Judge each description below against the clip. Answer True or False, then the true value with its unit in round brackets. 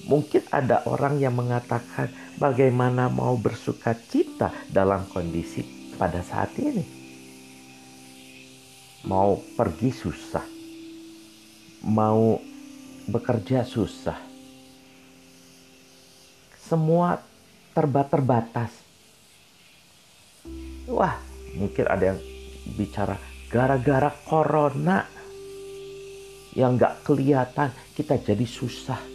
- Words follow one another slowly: True (70 wpm)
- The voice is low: True (125 Hz)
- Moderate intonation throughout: False (7.4 semitones)